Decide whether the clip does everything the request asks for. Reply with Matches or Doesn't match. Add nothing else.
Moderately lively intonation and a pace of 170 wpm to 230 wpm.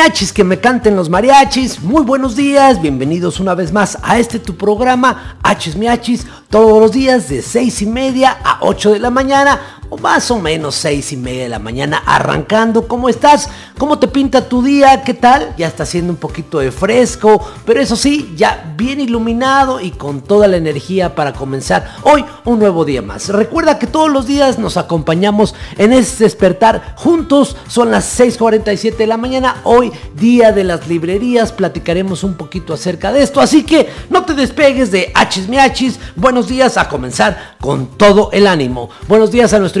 Doesn't match